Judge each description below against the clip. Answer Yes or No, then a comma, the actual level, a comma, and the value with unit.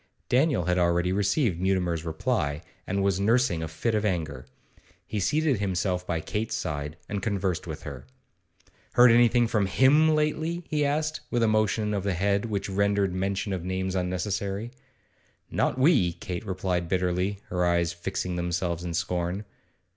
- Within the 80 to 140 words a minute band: No, average, 160 wpm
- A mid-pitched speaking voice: No, very low, 95 Hz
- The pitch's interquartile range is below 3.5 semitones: No, average, 3.8 semitones